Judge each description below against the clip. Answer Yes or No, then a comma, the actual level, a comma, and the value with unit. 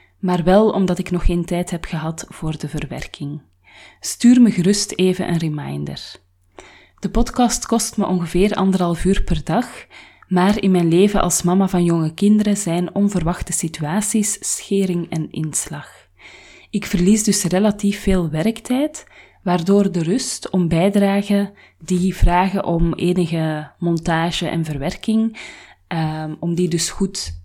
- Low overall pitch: No, medium, 180 Hz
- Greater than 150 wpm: No, average, 145 wpm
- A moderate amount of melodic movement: Yes, average, 3.3 semitones